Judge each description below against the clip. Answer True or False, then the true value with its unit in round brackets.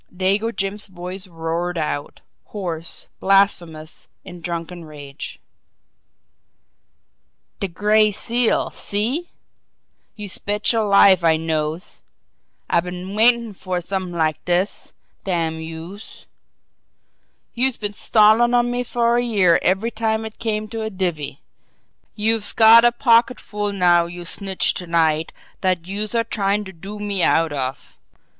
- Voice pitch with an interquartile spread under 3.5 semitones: False (4.3 semitones)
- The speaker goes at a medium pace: False (130 wpm)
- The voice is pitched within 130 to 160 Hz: False (195 Hz)